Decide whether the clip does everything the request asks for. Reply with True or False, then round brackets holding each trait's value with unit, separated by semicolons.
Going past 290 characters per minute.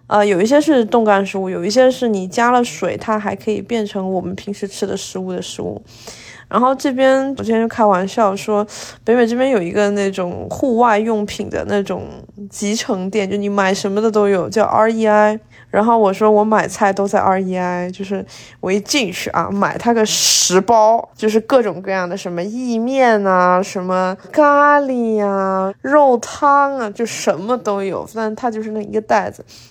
False (275 characters per minute)